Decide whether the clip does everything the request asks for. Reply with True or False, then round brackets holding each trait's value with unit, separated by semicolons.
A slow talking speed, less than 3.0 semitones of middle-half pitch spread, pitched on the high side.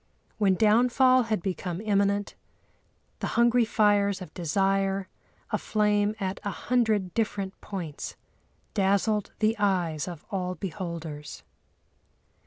True (105 wpm; 2.6 semitones; 200 Hz)